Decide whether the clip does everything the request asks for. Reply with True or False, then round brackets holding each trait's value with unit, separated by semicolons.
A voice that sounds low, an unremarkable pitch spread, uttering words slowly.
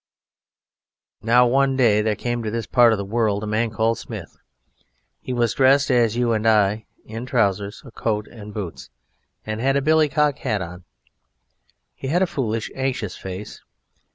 False (115 Hz; 3.3 semitones; 180 wpm)